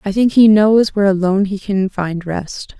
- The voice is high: Yes, high, 200 Hz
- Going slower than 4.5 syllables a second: No, 4.9 syllables/s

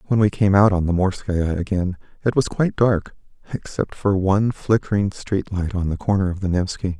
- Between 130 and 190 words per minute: No, fast, 205 wpm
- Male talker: Yes, male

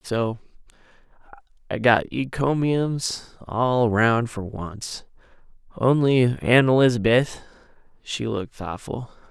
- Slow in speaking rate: Yes, slow, 85 wpm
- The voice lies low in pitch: Yes, low, 120 Hz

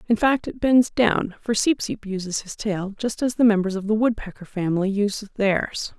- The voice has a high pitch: Yes, high, 210 Hz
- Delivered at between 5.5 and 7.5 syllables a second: No, 4.9 syllables/s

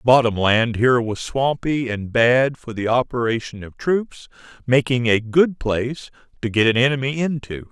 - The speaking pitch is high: No, low, 125 Hz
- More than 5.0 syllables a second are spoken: No, 4.8 syllables/s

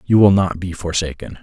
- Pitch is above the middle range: No, very low, 90 Hz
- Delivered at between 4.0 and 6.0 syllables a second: Yes, 5.5 syllables/s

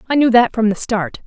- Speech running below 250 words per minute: No, fast, 285 wpm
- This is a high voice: Yes, high, 230 Hz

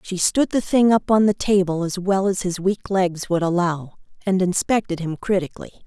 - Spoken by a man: No, female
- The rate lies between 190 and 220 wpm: Yes, fast, 205 wpm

